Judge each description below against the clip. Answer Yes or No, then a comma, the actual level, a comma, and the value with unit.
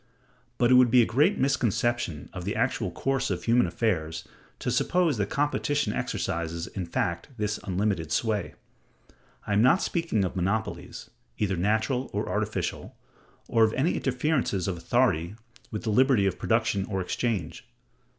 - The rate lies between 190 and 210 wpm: No, average, 155 wpm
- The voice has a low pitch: Yes, low, 110 Hz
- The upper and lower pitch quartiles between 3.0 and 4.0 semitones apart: No, average, 5.1 semitones